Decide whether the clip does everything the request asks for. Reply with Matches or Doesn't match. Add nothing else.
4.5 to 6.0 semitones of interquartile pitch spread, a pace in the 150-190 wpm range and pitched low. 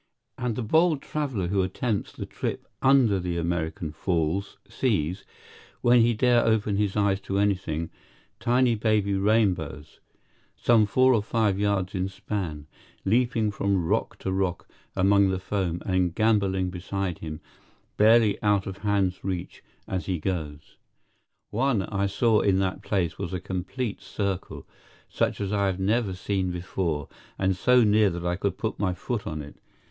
Doesn't match